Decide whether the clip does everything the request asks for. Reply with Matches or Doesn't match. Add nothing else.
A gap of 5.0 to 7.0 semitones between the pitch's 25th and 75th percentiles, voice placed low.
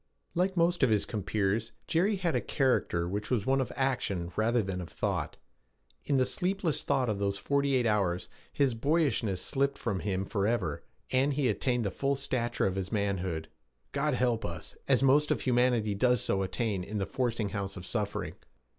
Matches